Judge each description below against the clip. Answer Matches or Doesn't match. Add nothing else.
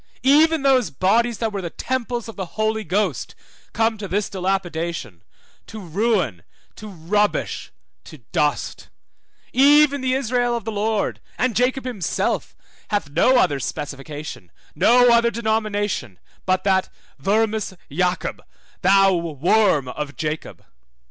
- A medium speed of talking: Doesn't match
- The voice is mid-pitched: Doesn't match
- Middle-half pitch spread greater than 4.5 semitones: Matches